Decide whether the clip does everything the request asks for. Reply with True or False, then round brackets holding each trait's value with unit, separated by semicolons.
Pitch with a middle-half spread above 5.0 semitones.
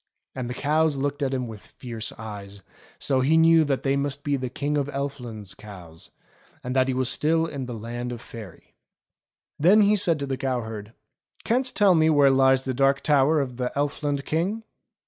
False (3.3 semitones)